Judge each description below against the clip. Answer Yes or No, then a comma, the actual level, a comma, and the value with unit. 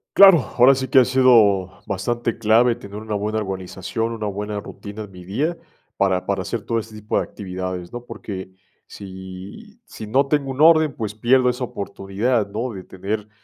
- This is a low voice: Yes, low, 110 Hz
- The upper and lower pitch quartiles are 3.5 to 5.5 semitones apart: Yes, average, 4.1 semitones